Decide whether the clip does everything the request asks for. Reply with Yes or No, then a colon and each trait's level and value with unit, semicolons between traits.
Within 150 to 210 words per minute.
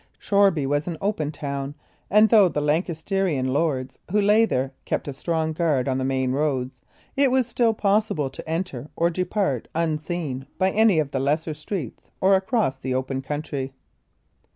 Yes: average, 170 wpm